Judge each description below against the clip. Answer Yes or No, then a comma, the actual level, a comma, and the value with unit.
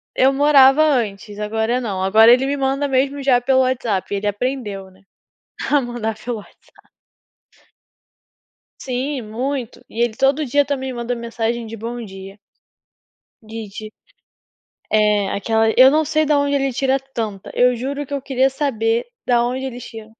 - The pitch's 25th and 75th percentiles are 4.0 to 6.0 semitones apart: No, average, 3.5 semitones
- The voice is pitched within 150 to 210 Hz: No, high, 245 Hz